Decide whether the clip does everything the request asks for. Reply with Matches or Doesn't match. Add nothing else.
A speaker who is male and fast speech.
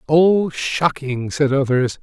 Doesn't match